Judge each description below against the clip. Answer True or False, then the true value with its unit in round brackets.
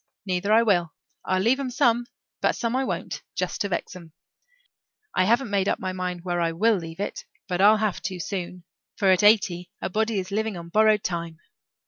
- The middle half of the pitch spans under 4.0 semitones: True (3.6 semitones)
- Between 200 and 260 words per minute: True (205 wpm)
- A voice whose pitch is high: True (195 Hz)